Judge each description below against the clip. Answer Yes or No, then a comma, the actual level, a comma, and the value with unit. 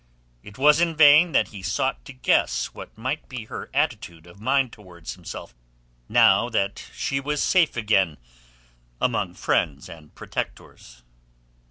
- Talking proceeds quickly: No, average, 145 wpm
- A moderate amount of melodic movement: No, wide, 8.3 semitones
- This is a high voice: No, low, 110 Hz